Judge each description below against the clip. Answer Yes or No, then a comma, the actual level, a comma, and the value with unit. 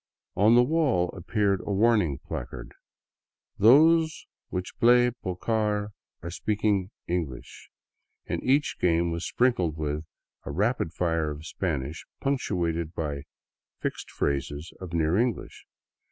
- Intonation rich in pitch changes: Yes, wide, 6.1 semitones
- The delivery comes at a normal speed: No, slow, 125 wpm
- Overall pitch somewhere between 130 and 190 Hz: No, very low, 90 Hz